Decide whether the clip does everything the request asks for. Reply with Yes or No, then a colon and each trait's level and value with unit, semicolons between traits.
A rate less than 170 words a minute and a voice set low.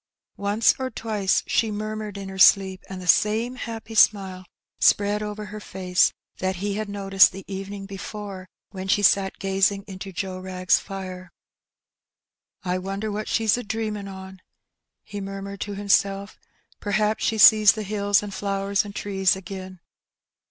No: average, 155 wpm; high, 200 Hz